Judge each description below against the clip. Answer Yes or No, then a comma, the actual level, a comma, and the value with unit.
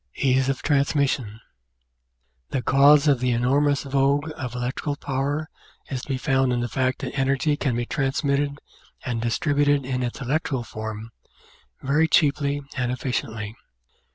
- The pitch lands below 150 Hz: Yes, low, 135 Hz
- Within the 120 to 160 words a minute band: Yes, average, 145 wpm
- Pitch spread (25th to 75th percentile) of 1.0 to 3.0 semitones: Yes, narrow, 2.4 semitones